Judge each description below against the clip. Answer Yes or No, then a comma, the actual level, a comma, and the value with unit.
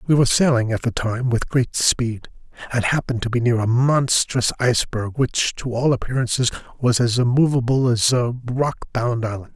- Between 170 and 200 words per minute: Yes, average, 175 wpm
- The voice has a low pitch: Yes, low, 120 Hz